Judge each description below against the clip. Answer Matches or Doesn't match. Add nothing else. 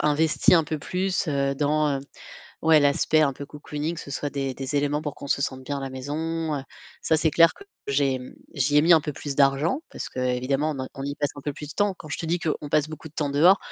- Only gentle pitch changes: Matches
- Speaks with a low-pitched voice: Doesn't match